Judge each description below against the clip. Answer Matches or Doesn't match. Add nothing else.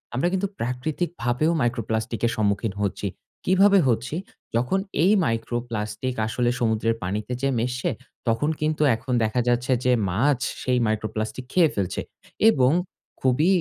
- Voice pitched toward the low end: Matches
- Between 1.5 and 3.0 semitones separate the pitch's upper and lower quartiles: Doesn't match